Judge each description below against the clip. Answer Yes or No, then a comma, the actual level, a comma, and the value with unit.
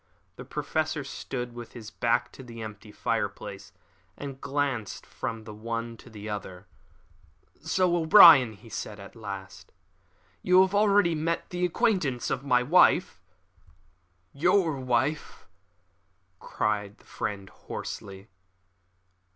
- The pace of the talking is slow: Yes, slow, 120 wpm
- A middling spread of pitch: No, wide, 6.5 semitones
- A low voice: Yes, low, 125 Hz